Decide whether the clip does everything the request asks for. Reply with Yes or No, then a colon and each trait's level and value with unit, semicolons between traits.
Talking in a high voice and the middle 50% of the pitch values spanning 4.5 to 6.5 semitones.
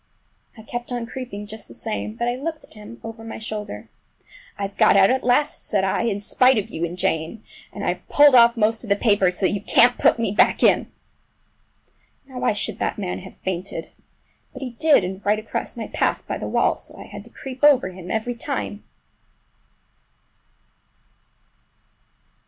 No: high, 220 Hz; average, 3.5 semitones